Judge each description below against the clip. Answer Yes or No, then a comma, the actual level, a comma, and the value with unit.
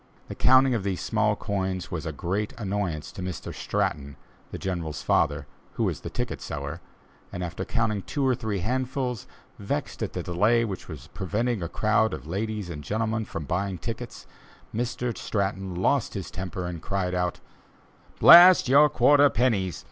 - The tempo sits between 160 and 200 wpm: Yes, average, 165 wpm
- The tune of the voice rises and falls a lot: No, average, 4.7 semitones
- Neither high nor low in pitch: No, low, 100 Hz